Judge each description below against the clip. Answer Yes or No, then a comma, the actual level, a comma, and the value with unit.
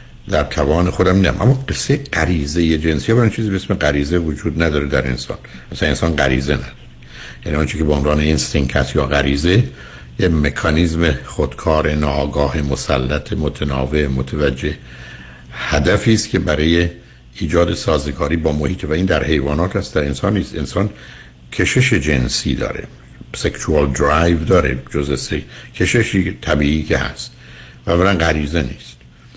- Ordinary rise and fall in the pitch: Yes, average, 3.8 semitones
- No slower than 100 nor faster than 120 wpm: No, average, 140 wpm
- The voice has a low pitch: Yes, very low, 75 Hz